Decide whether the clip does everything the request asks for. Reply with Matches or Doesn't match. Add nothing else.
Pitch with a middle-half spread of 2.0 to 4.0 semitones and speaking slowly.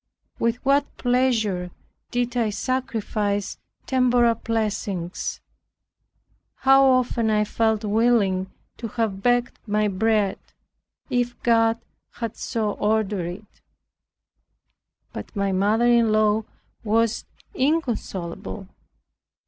Matches